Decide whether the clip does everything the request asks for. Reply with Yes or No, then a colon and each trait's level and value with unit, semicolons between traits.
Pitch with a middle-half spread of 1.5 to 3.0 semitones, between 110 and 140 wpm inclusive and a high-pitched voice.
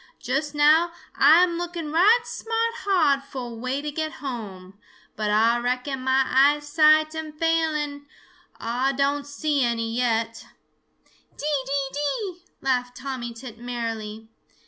No: average, 4.1 semitones; slow, 135 wpm; very high, 275 Hz